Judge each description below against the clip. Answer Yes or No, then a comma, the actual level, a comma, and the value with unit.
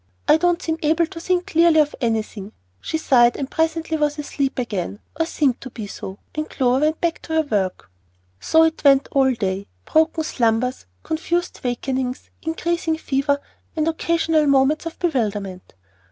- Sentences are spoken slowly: No, average, 165 wpm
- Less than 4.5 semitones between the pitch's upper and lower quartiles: No, average, 4.8 semitones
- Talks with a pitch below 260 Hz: No, very high, 295 Hz